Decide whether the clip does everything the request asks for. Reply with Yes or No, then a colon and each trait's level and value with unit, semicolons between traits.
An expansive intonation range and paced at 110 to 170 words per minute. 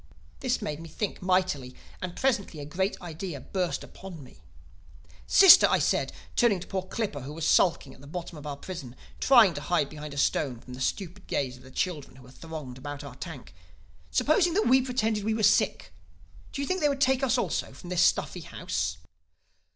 No: wide, 7.1 semitones; average, 200 wpm